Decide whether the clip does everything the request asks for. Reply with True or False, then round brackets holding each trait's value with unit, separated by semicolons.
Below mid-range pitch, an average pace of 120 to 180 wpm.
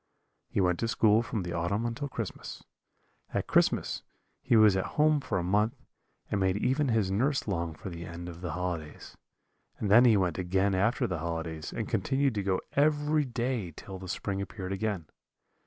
False (100 Hz; 190 wpm)